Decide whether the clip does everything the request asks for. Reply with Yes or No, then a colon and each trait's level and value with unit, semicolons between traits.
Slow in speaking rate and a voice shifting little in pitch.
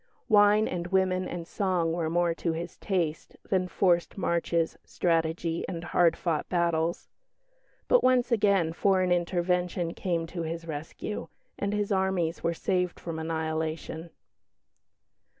Yes: slow, 130 wpm; narrow, 2.3 semitones